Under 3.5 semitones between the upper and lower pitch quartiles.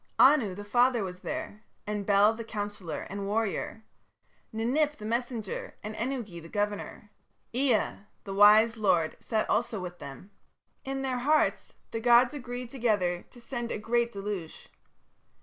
Yes: average, 3.1 semitones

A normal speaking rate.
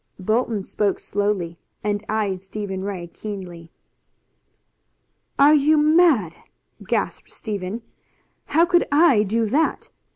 No: slow, 105 wpm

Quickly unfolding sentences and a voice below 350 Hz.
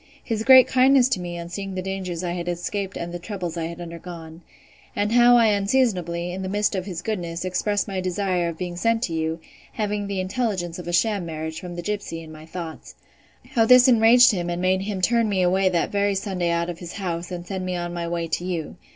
Yes: fast, 230 wpm; medium, 185 Hz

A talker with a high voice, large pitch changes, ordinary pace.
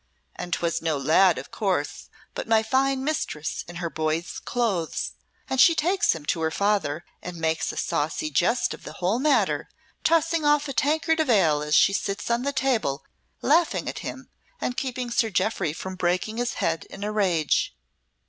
Yes: high, 195 Hz; wide, 8.0 semitones; average, 185 wpm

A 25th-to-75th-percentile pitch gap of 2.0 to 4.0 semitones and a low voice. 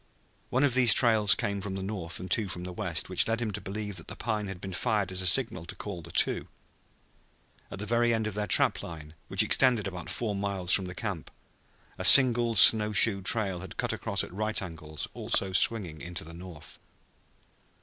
Yes: average, 3.5 semitones; low, 100 Hz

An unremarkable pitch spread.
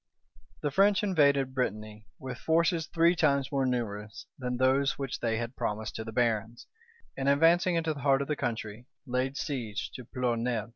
Yes: average, 3.7 semitones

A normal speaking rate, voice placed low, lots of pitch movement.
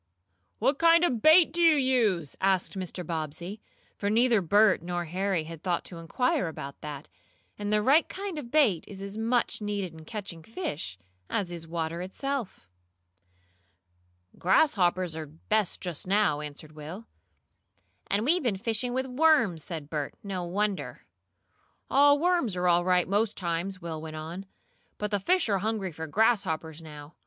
No: average, 160 wpm; high, 195 Hz; wide, 5.7 semitones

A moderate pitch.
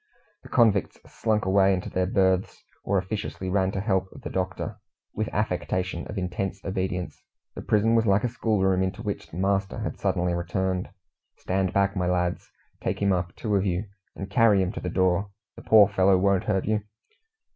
No: very low, 95 Hz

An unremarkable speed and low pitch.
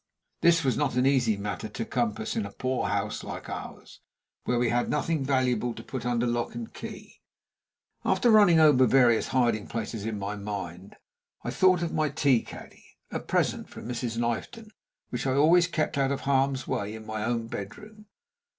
Yes: average, 185 wpm; low, 125 Hz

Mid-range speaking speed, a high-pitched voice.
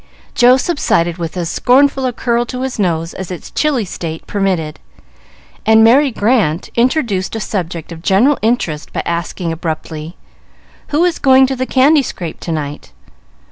Yes: average, 160 wpm; high, 205 Hz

